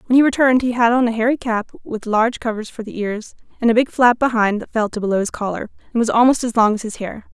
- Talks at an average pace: No, fast, 275 wpm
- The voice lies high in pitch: Yes, high, 230 Hz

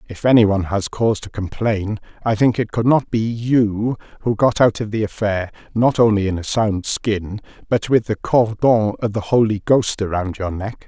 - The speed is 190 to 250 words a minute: Yes, fast, 205 wpm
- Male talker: Yes, male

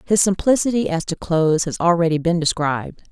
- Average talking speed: Yes, average, 175 wpm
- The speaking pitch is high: No, medium, 170 Hz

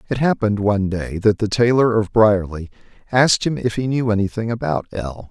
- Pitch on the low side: Yes, low, 105 Hz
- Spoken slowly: No, fast, 205 wpm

